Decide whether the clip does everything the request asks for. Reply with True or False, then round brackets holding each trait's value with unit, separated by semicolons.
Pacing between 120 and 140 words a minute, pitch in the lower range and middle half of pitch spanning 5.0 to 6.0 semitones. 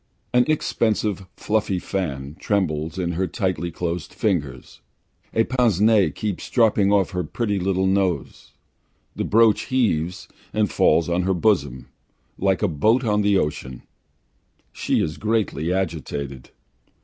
False (135 wpm; 95 Hz; 4.2 semitones)